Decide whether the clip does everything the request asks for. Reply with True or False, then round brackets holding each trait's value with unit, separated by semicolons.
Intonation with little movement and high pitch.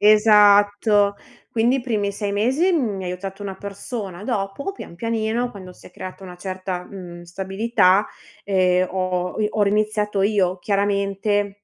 True (2.2 semitones; 200 Hz)